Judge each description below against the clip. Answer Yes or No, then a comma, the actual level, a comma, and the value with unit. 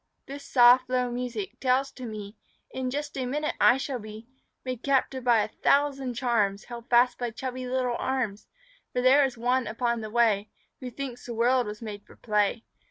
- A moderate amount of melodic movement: No, narrow, 2.3 semitones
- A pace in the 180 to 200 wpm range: Yes, average, 190 wpm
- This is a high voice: Yes, high, 245 Hz